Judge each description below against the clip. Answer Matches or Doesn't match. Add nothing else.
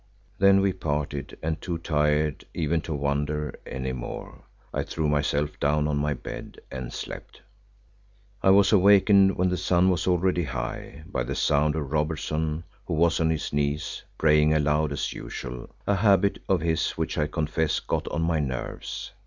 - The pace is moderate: Matches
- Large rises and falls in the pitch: Doesn't match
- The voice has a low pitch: Matches